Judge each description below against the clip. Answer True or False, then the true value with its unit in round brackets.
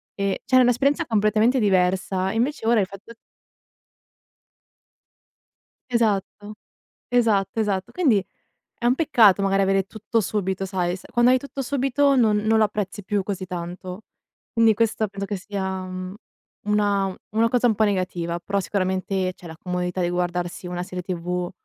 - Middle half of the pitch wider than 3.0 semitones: True (3.5 semitones)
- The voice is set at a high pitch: True (200 Hz)